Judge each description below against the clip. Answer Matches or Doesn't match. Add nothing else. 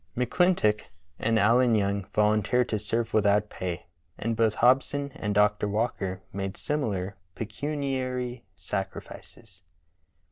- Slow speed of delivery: Matches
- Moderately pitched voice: Doesn't match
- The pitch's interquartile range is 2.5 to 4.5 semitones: Matches